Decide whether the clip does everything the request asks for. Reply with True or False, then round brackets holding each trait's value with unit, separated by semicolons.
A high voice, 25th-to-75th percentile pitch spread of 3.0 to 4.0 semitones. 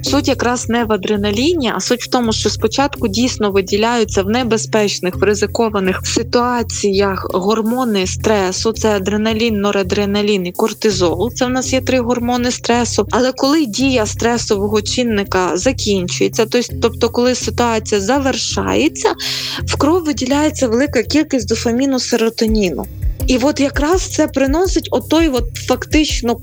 True (235 Hz; 3.6 semitones)